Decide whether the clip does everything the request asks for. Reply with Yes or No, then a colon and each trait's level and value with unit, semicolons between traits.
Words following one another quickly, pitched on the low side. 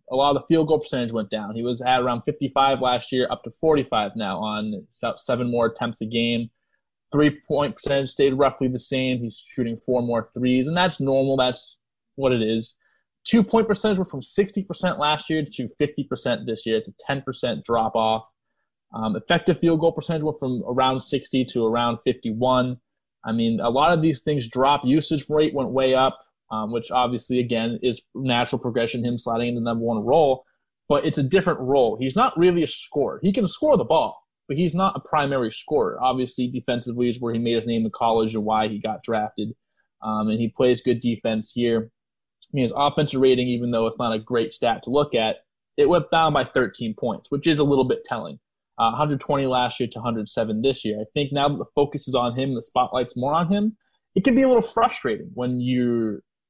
Yes: fast, 215 wpm; low, 125 Hz